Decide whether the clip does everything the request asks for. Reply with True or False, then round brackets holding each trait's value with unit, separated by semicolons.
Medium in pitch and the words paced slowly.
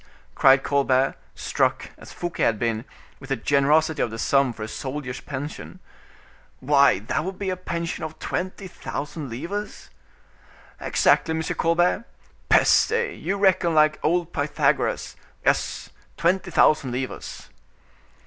True (155 Hz; 130 wpm)